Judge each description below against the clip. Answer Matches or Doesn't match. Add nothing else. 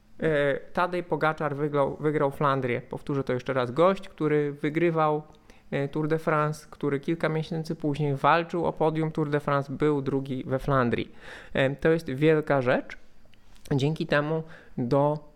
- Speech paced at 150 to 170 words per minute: Doesn't match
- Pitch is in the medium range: Matches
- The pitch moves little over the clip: Matches